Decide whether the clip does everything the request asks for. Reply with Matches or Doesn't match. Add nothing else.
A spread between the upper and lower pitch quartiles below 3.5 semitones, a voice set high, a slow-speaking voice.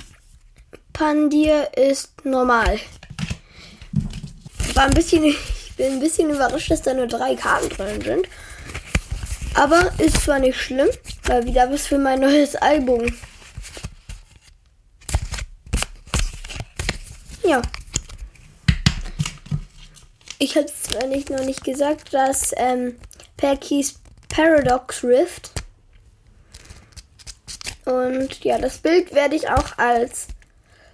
Matches